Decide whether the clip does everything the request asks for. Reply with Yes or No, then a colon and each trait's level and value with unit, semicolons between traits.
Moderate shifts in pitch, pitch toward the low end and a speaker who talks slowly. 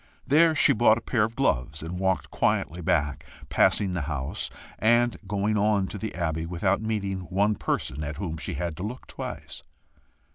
No: average, 5.0 semitones; very low, 95 Hz; average, 180 wpm